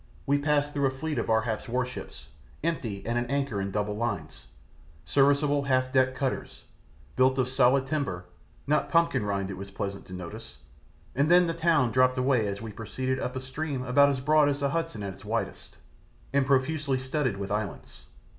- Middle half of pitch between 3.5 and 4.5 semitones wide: Yes, average, 4.2 semitones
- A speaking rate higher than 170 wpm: Yes, average, 190 wpm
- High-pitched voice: No, low, 130 Hz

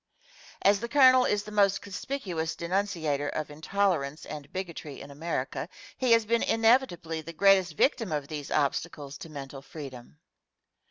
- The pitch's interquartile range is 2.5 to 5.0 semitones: No, wide, 5.6 semitones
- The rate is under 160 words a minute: Yes, average, 150 wpm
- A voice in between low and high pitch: Yes, medium, 170 Hz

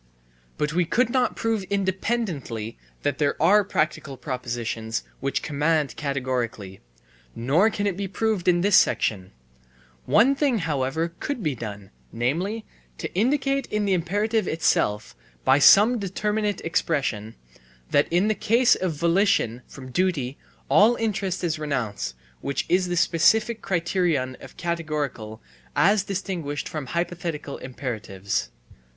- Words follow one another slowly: Yes, slow, 130 wpm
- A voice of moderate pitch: Yes, medium, 165 Hz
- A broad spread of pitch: Yes, wide, 7.3 semitones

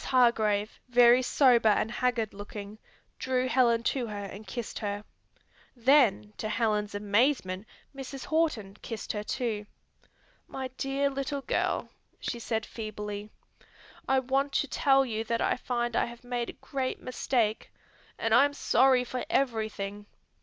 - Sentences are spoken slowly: No, average, 145 wpm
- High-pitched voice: Yes, high, 235 Hz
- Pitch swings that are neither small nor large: Yes, average, 3.6 semitones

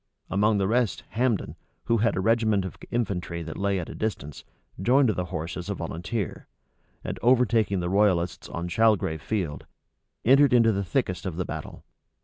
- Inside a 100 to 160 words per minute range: No, average, 170 wpm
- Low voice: Yes, low, 100 Hz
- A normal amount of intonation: Yes, average, 4.4 semitones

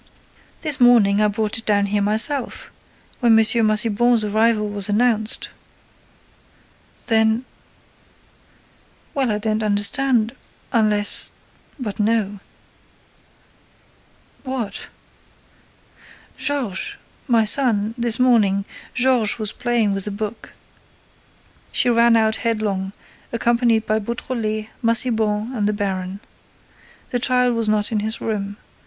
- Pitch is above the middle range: Yes, high, 220 Hz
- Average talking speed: No, slow, 100 wpm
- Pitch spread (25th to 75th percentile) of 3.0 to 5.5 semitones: No, narrow, 2.4 semitones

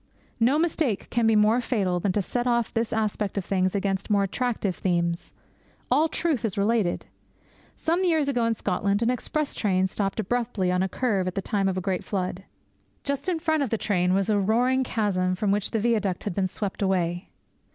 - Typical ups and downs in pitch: Yes, average, 4.2 semitones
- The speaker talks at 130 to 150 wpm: No, fast, 205 wpm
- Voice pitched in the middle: No, high, 210 Hz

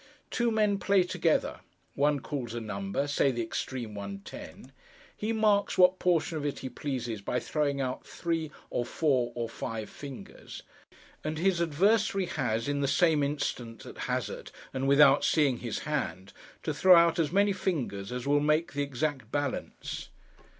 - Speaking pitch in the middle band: Yes, medium, 145 Hz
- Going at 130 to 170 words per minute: Yes, average, 165 wpm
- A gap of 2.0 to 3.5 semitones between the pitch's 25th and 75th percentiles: No, wide, 5.5 semitones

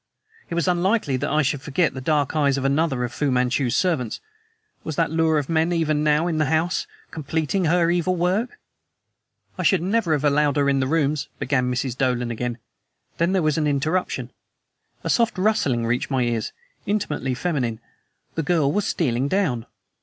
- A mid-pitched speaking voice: Yes, medium, 150 Hz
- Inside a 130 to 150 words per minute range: No, average, 185 wpm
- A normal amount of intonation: Yes, average, 4.4 semitones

